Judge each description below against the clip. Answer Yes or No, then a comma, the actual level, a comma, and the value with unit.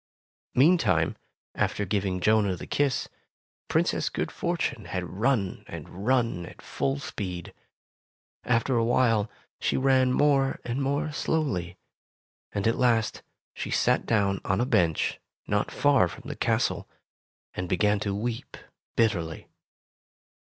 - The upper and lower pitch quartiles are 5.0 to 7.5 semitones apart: Yes, wide, 5.6 semitones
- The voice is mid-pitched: No, low, 110 Hz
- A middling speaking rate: No, slow, 130 wpm